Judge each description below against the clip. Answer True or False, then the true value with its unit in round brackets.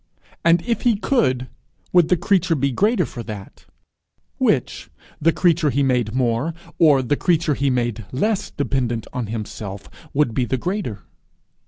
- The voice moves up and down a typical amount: False (6.2 semitones)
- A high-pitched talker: False (140 Hz)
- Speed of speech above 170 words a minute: False (160 wpm)